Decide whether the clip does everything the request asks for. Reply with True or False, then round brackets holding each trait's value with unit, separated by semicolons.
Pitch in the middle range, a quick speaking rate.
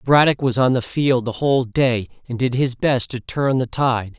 False (125 Hz; 245 wpm)